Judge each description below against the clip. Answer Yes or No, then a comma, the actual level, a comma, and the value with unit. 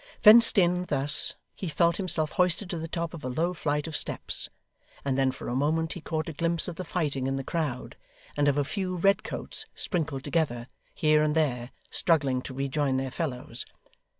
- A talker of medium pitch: Yes, medium, 155 Hz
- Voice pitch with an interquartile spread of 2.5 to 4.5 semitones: Yes, average, 3.9 semitones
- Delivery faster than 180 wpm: Yes, average, 200 wpm